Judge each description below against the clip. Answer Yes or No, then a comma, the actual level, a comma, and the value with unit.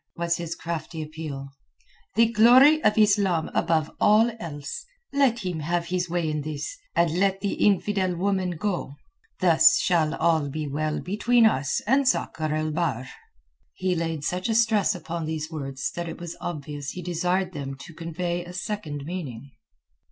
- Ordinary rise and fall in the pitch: Yes, average, 4.2 semitones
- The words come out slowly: No, average, 165 wpm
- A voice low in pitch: No, medium, 170 Hz